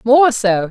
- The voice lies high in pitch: Yes, high, 230 Hz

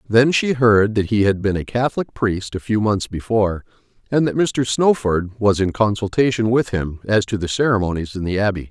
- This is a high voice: No, low, 110 Hz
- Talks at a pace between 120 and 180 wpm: No, fast, 205 wpm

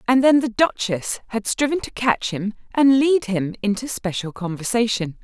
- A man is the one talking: No, female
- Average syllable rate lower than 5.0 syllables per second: Yes, 4.7 syllables/s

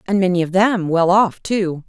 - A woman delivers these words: Yes, female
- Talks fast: Yes, fast, 225 wpm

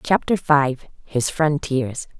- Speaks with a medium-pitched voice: Yes, medium, 145 Hz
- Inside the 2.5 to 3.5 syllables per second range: Yes, 3.2 syllables/s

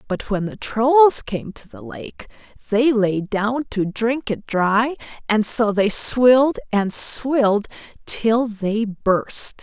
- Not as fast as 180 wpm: Yes, average, 150 wpm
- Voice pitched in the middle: No, high, 225 Hz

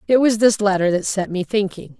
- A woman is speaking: Yes, female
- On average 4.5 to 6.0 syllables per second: Yes, 5.5 syllables/s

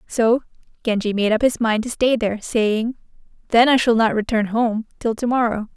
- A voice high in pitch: Yes, high, 225 Hz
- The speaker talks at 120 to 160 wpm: No, average, 200 wpm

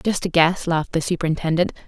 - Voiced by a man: No, female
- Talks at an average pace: Yes, average, 190 wpm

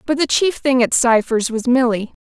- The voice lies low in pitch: No, very high, 250 Hz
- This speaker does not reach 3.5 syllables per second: No, 4.9 syllables/s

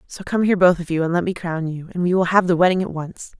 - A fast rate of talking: Yes, fast, 335 wpm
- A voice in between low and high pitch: Yes, medium, 175 Hz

